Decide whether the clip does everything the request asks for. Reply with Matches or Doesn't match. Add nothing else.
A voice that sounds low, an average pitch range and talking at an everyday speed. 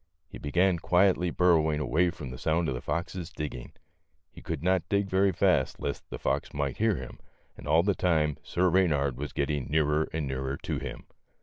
Matches